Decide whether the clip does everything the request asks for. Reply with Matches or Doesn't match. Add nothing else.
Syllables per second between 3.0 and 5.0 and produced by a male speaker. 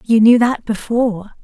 Doesn't match